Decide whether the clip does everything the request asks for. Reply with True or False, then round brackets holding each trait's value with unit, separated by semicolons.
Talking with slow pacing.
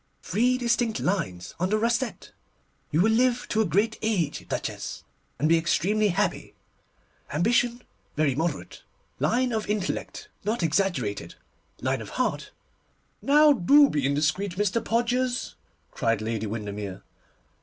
True (125 wpm)